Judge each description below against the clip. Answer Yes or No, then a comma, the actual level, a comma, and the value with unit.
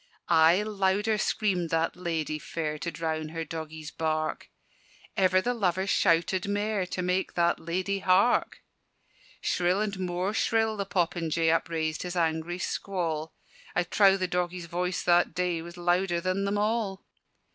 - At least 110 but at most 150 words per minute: Yes, average, 145 wpm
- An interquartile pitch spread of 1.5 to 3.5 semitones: Yes, average, 2.8 semitones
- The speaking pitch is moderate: Yes, medium, 180 Hz